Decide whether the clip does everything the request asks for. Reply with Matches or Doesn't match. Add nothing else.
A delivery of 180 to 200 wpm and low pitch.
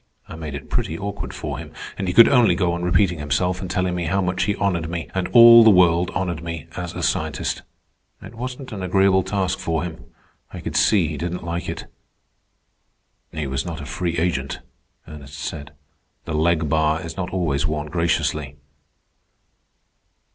Matches